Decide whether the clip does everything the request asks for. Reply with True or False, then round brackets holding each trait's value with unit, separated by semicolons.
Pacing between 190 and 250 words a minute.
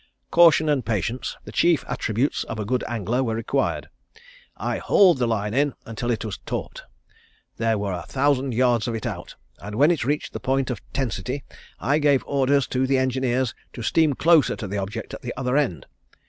True (195 wpm)